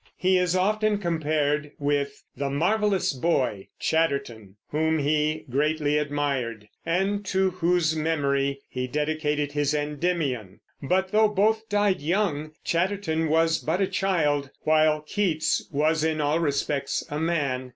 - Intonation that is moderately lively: Yes, average, 3.7 semitones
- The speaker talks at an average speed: No, slow, 130 wpm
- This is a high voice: No, medium, 155 Hz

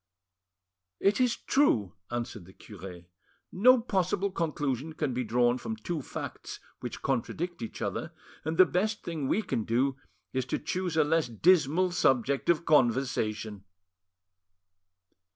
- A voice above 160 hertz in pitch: No, medium, 150 Hz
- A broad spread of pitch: Yes, wide, 7.0 semitones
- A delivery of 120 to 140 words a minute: Yes, slow, 135 wpm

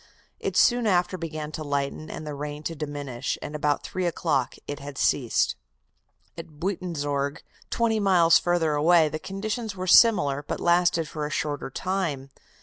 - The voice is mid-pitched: Yes, medium, 155 Hz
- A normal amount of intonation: Yes, average, 3.6 semitones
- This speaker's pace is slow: No, average, 160 wpm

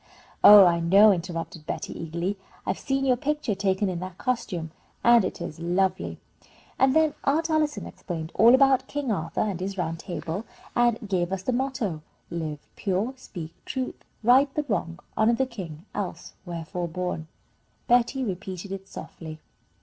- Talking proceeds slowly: No, average, 160 wpm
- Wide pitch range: Yes, wide, 6.2 semitones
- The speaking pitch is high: Yes, high, 195 Hz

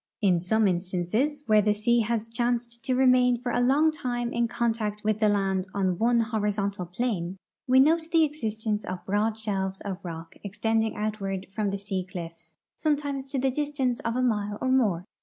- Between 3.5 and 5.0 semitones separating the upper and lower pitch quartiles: Yes, average, 4.1 semitones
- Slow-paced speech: No, average, 185 wpm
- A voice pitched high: Yes, high, 220 Hz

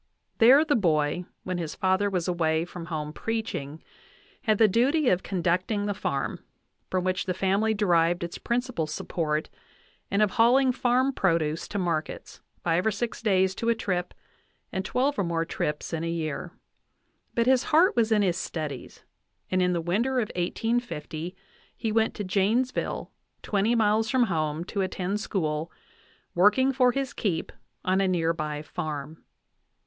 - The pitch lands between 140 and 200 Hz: Yes, high, 190 Hz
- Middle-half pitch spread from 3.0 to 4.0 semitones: No, average, 5.2 semitones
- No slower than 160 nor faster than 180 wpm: Yes, average, 165 wpm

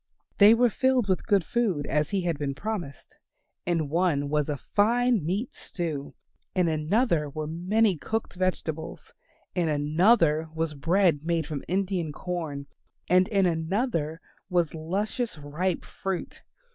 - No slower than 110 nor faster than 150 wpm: Yes, average, 140 wpm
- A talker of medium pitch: Yes, medium, 175 Hz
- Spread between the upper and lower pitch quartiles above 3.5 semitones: Yes, average, 4.6 semitones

